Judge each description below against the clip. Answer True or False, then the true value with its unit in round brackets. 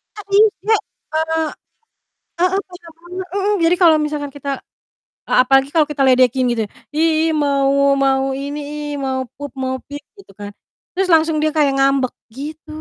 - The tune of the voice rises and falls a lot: False (3.6 semitones)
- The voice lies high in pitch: True (295 Hz)